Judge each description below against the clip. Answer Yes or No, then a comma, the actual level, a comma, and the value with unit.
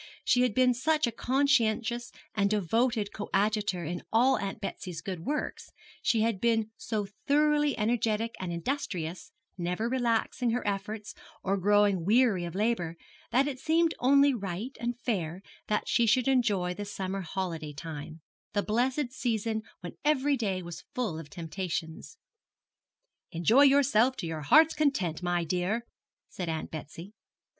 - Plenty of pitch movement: Yes, wide, 5.7 semitones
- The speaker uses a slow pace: No, average, 150 wpm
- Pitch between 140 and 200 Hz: No, high, 215 Hz